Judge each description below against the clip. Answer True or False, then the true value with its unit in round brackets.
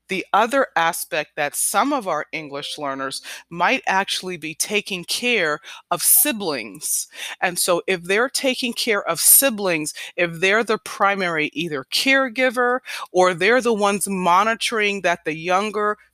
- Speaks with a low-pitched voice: False (190 Hz)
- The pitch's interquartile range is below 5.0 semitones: False (5.3 semitones)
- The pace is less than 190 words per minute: True (140 wpm)